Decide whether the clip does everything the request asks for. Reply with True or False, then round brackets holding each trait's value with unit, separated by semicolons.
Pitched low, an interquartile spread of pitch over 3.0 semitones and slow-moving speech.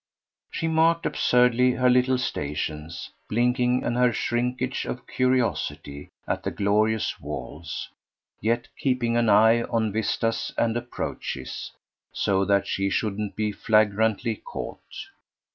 True (115 Hz; 3.4 semitones; 120 wpm)